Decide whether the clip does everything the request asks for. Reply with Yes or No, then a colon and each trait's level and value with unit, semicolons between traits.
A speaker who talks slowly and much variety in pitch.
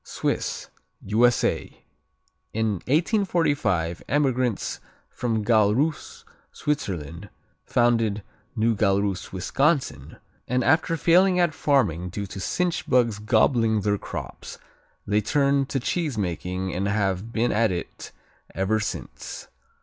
Yes: slow, 105 wpm; wide, 5.9 semitones